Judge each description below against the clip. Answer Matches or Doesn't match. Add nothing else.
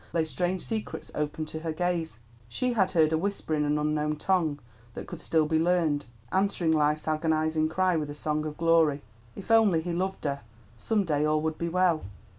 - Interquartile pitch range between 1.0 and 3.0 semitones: Matches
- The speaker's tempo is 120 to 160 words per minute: Doesn't match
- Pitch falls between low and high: Matches